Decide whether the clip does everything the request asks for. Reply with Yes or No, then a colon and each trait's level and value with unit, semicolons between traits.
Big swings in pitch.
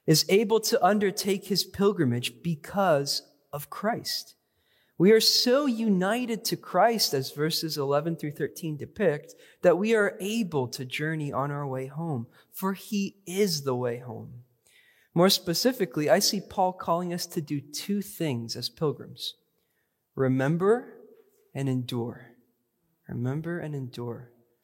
Yes: wide, 7.1 semitones